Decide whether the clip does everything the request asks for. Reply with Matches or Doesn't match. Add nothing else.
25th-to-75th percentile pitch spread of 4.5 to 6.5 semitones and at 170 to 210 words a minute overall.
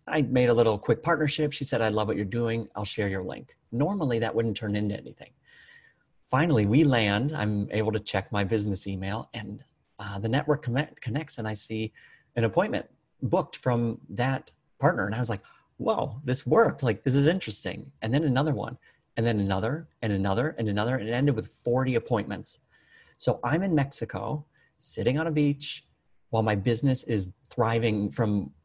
Matches